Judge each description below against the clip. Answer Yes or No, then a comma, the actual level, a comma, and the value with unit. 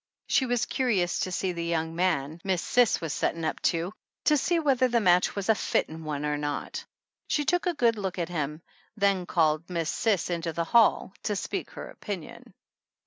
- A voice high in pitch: No, medium, 180 Hz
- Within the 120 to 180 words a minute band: No, average, 195 wpm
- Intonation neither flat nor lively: No, wide, 5.7 semitones